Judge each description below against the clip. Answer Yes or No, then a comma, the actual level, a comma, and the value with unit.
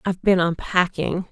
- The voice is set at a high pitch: No, medium, 180 Hz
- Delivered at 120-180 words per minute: Yes, slow, 135 wpm